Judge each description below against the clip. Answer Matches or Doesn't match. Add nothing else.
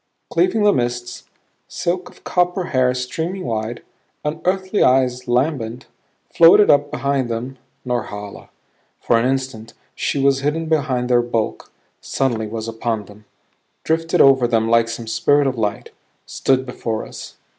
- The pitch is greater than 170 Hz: Doesn't match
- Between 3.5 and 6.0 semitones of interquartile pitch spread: Matches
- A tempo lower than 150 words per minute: Matches